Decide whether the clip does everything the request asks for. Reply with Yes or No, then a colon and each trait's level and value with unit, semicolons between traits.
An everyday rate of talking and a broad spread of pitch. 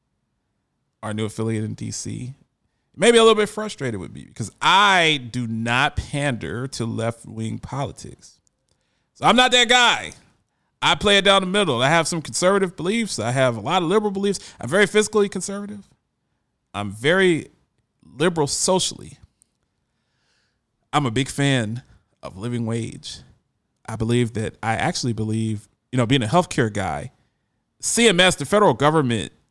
Yes: average, 150 wpm; wide, 8.7 semitones